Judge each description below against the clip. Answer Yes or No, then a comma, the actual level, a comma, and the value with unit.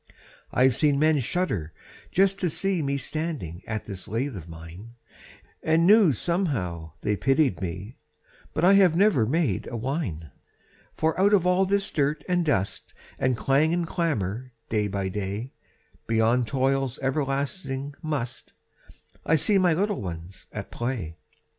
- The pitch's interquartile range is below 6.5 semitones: No, wide, 7.9 semitones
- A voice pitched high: No, low, 135 Hz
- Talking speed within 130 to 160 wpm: Yes, average, 145 wpm